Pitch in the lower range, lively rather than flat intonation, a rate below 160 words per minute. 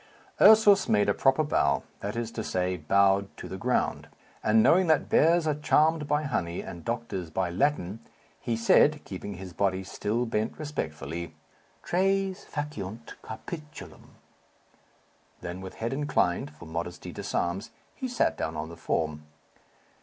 Yes: low, 110 Hz; wide, 9.0 semitones; average, 145 wpm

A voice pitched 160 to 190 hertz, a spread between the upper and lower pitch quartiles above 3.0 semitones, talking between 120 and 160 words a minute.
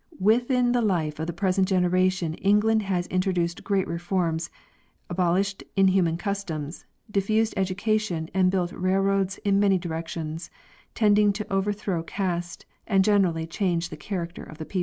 No: medium, 185 Hz; average, 2.7 semitones; average, 155 wpm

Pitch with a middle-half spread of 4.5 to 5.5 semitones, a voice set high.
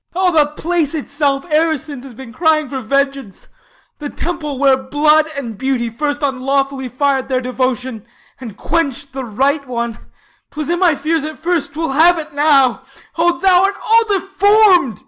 No: average, 3.7 semitones; very high, 285 Hz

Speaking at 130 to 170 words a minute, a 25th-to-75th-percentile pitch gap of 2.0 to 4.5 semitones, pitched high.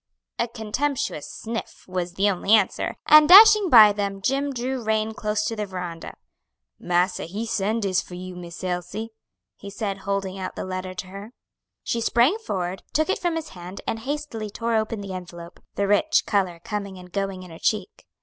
No: average, 190 wpm; average, 3.8 semitones; high, 205 Hz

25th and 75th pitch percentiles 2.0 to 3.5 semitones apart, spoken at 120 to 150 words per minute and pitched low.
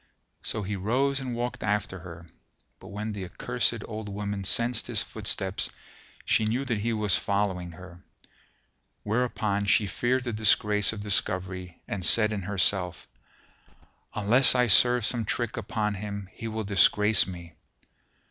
Yes: average, 2.8 semitones; average, 145 wpm; low, 105 Hz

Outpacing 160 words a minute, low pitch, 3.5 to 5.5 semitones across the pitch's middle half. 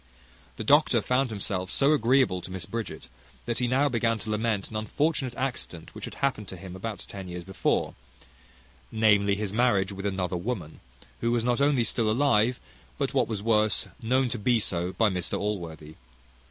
Yes: average, 180 wpm; low, 110 Hz; average, 4.2 semitones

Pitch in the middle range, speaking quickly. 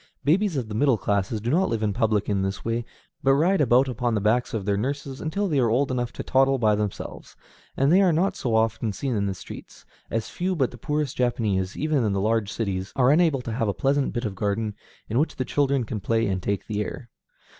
No: low, 120 Hz; fast, 240 wpm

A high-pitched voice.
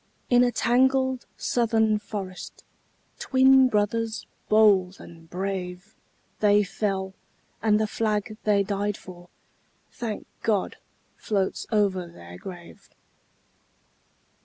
Yes: high, 210 Hz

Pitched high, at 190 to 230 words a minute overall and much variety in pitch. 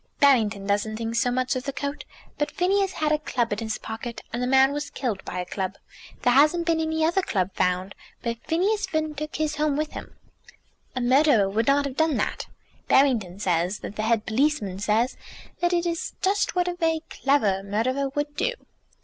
Yes: very high, 265 Hz; average, 200 wpm; wide, 6.0 semitones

